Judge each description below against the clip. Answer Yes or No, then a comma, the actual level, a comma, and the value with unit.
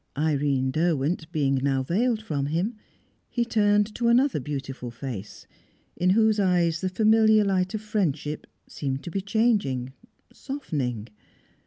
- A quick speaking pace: No, slow, 135 wpm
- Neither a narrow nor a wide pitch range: No, wide, 7.7 semitones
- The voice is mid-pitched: Yes, medium, 175 Hz